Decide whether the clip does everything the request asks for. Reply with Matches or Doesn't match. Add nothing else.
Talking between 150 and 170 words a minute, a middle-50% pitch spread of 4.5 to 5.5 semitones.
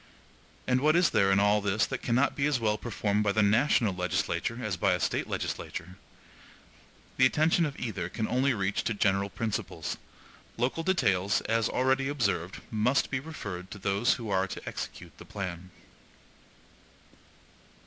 Matches